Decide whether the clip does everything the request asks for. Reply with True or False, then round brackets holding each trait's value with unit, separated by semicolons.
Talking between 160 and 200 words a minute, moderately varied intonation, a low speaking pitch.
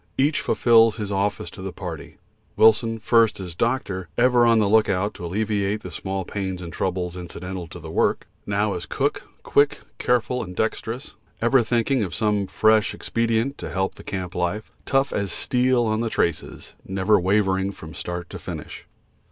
True (175 wpm; 3.5 semitones; 105 Hz)